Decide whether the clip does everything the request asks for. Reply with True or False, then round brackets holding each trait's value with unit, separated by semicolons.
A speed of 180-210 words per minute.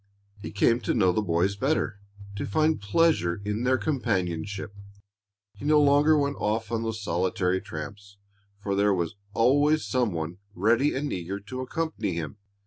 False (160 wpm)